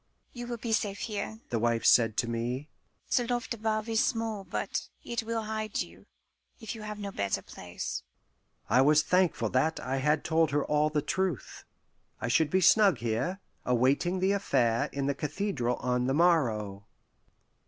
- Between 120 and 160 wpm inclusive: No, average, 175 wpm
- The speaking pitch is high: No, medium, 155 Hz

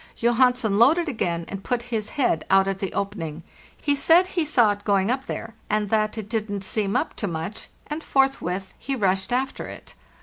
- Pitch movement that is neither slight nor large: Yes, average, 4.8 semitones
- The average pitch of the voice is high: Yes, high, 215 Hz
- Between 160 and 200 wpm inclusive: Yes, average, 195 wpm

